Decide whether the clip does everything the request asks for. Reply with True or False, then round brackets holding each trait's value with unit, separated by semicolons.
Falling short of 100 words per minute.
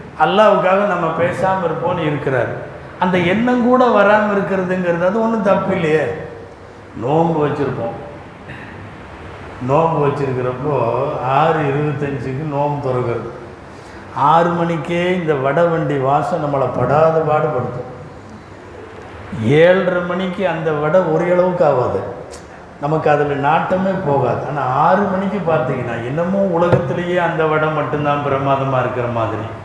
False (105 wpm)